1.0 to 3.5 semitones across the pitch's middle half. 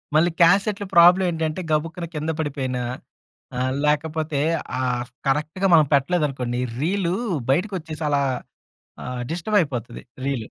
No: average, 3.9 semitones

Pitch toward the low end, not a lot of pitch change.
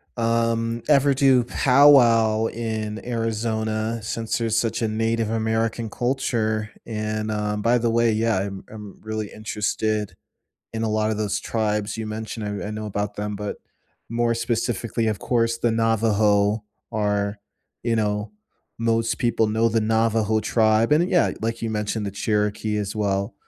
Yes: low, 110 Hz; narrow, 1.4 semitones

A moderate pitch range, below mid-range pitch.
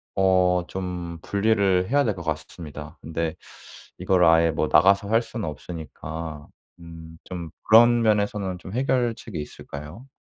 Yes: average, 4.0 semitones; very low, 90 Hz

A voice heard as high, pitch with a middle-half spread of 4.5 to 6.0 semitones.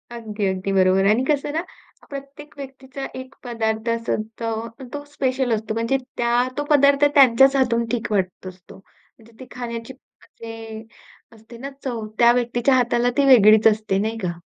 No: high, 235 Hz; average, 3.3 semitones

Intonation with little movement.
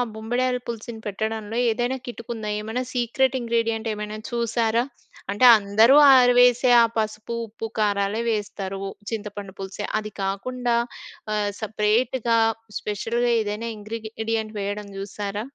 Yes: narrow, 2.1 semitones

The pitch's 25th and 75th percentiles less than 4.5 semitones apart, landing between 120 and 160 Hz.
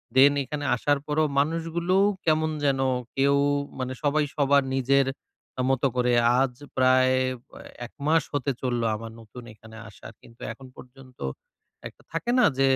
Yes: average, 2.7 semitones; low, 135 Hz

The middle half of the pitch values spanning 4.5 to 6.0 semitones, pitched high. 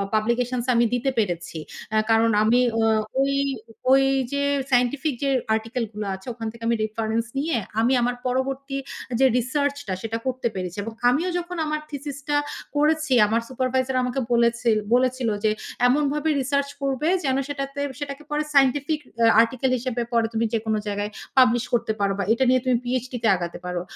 No: average, 3.3 semitones; very high, 250 Hz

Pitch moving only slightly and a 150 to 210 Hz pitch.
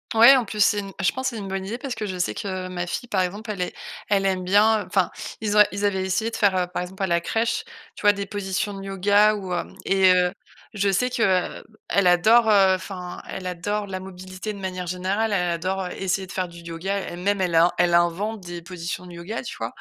Yes: narrow, 2.3 semitones; high, 190 Hz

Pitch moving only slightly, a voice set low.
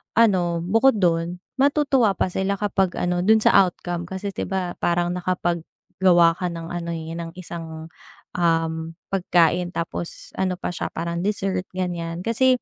No: narrow, 2.2 semitones; medium, 175 Hz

